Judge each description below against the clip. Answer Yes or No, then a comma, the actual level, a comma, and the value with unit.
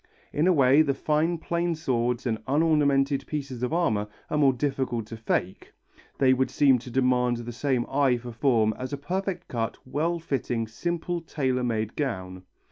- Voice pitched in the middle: No, low, 130 Hz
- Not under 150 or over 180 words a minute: Yes, average, 175 wpm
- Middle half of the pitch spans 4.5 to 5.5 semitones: No, average, 4.0 semitones